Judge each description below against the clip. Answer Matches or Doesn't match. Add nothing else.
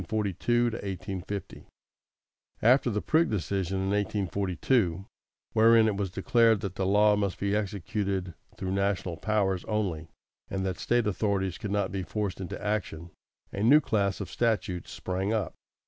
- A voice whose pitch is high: Doesn't match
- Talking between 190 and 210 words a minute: Doesn't match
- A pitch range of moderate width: Doesn't match